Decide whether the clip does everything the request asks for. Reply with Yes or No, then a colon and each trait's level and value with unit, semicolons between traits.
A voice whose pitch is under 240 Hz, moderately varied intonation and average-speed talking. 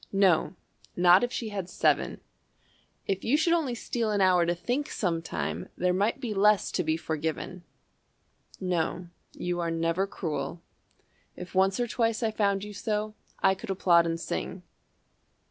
Yes: high, 190 Hz; average, 3.7 semitones; average, 160 wpm